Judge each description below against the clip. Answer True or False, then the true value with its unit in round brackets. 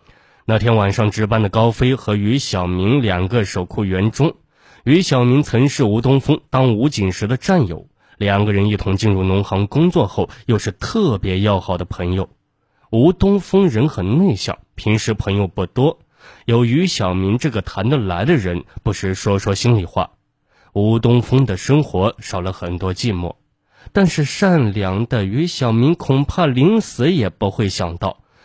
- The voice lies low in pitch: True (110 Hz)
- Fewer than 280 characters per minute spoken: True (245 characters per minute)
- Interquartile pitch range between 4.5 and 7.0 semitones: True (5.6 semitones)